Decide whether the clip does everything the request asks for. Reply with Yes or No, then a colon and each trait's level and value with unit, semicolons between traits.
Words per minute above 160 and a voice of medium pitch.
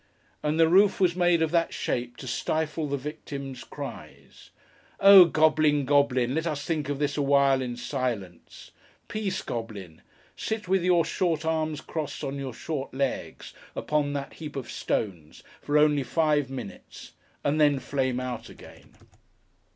No: average, 150 wpm; medium, 145 Hz